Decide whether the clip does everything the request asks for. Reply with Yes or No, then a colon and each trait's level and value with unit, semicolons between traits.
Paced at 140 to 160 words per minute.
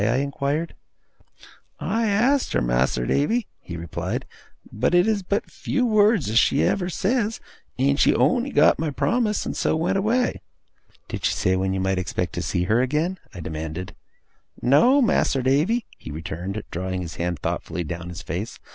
No: average, 175 wpm